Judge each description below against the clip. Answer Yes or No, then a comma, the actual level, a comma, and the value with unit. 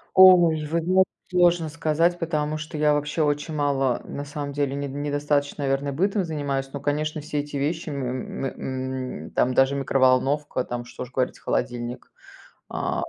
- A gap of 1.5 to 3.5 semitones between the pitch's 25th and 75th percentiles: Yes, narrow, 2.4 semitones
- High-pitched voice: No, medium, 145 Hz